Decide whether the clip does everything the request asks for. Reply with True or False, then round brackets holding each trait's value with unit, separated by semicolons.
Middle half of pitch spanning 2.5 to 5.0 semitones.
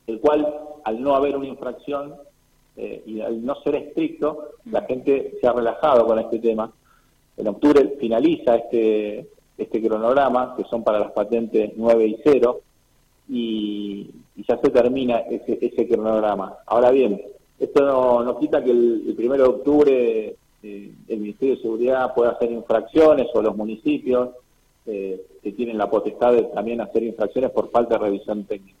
True (4.3 semitones)